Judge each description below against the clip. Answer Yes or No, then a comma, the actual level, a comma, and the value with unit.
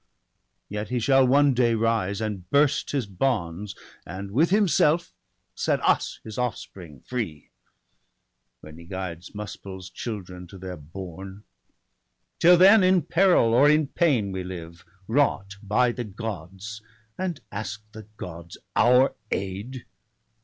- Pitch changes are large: Yes, wide, 5.9 semitones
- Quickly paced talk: No, slow, 135 wpm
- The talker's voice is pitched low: Yes, low, 105 Hz